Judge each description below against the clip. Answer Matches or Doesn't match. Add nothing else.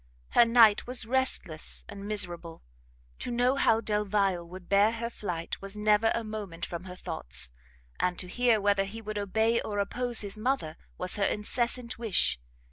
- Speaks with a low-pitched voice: Doesn't match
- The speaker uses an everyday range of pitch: Matches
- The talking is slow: Doesn't match